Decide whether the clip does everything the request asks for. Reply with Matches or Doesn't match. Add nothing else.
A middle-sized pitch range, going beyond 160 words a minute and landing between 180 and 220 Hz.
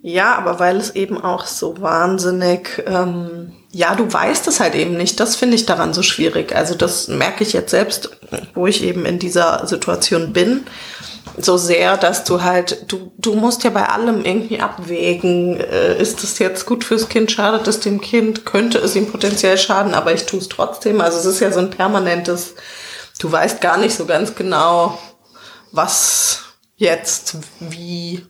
Matches